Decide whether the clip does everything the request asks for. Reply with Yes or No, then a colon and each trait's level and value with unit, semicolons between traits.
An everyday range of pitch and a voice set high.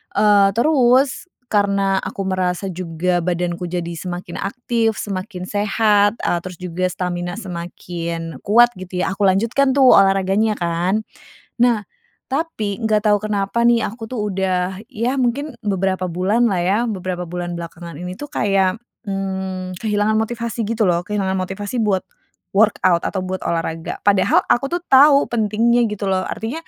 Yes: average, 3.5 semitones; high, 195 Hz